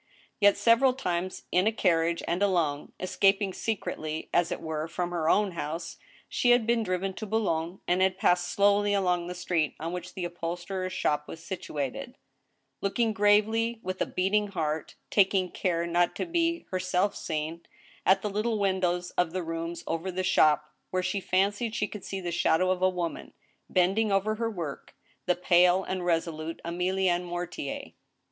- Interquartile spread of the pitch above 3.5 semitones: No, average, 2.9 semitones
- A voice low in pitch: No, medium, 185 Hz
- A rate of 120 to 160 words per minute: No, average, 170 wpm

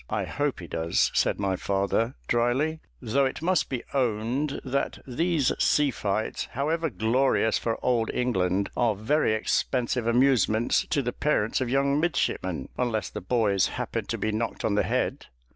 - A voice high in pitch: No, low, 120 Hz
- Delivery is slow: No, average, 160 wpm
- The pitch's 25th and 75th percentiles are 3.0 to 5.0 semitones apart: Yes, average, 4.3 semitones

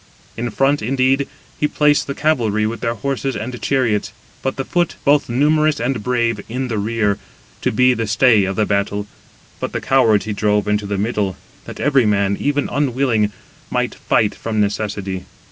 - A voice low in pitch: Yes, low, 115 Hz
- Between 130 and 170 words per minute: No, average, 180 wpm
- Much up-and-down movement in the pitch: No, average, 4.4 semitones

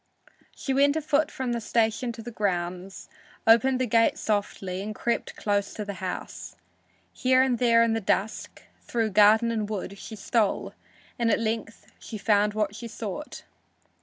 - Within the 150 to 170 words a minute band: Yes, average, 165 wpm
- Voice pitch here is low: No, high, 220 Hz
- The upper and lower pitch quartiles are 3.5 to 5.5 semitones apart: No, narrow, 2.6 semitones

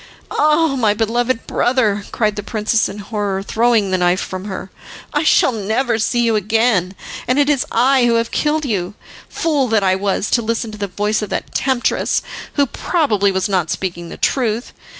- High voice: Yes, high, 220 Hz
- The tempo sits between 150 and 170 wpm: No, average, 190 wpm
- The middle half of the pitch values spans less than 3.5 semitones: No, average, 3.8 semitones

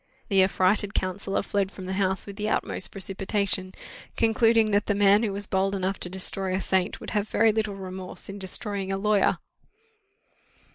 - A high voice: Yes, high, 195 Hz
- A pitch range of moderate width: No, narrow, 1.5 semitones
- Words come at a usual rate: Yes, average, 180 wpm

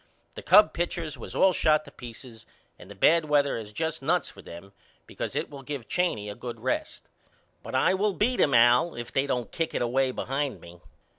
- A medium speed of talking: No, fast, 210 wpm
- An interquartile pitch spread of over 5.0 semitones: Yes, wide, 5.6 semitones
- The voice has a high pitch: No, low, 135 Hz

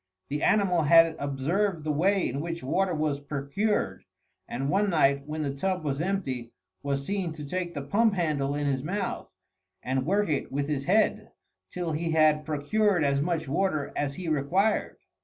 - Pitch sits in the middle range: Yes, medium, 155 Hz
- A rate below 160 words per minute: No, average, 175 wpm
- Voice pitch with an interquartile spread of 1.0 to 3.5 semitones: No, average, 4.7 semitones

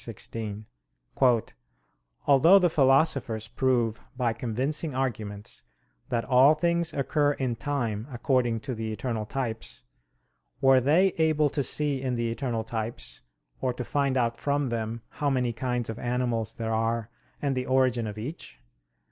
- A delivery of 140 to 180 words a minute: Yes, average, 150 wpm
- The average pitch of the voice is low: Yes, low, 125 Hz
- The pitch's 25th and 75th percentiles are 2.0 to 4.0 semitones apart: Yes, average, 3.5 semitones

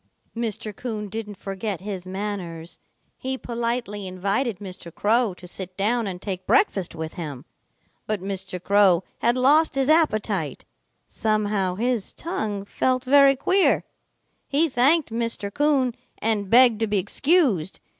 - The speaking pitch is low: No, high, 210 Hz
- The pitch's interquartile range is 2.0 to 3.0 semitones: No, average, 4.8 semitones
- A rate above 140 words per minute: No, slow, 135 wpm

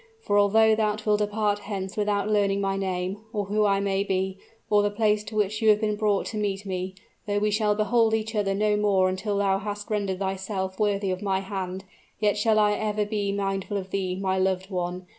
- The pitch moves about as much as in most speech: No, narrow, 1.6 semitones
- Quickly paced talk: Yes, fast, 215 wpm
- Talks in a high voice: Yes, high, 205 Hz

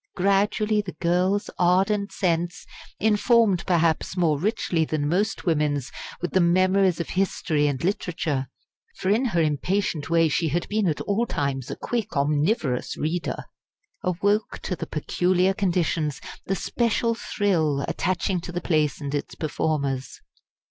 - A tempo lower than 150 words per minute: Yes, average, 140 wpm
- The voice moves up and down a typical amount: Yes, average, 4.4 semitones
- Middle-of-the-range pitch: Yes, medium, 175 Hz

